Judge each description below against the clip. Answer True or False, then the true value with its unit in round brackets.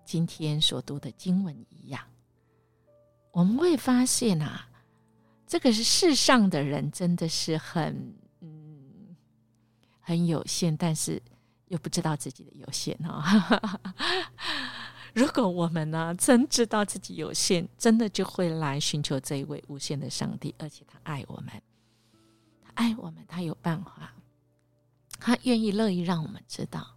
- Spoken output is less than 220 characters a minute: True (210 characters per minute)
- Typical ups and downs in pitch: False (6.7 semitones)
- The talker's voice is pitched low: False (160 Hz)